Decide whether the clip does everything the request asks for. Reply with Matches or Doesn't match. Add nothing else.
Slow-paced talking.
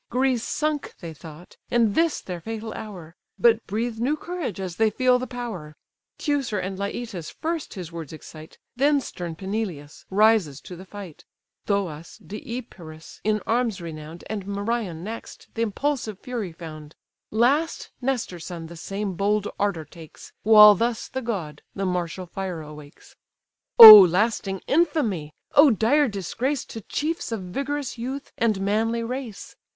Doesn't match